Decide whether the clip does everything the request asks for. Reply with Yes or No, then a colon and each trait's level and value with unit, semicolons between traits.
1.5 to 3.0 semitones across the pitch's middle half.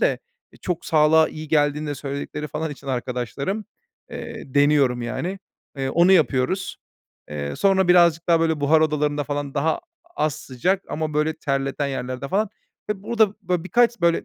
No: average, 4.2 semitones